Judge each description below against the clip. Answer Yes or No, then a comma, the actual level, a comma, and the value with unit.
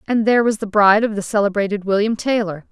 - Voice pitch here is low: No, high, 210 Hz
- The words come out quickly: Yes, fast, 220 wpm